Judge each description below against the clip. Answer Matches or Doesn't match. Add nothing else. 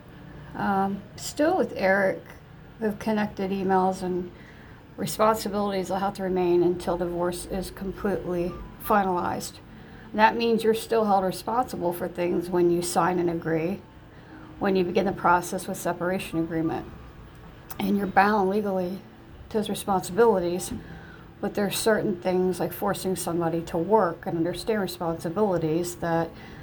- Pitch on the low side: Doesn't match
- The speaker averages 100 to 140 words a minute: Matches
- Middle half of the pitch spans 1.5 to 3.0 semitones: Matches